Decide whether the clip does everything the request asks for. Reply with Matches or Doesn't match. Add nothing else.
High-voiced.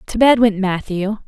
Matches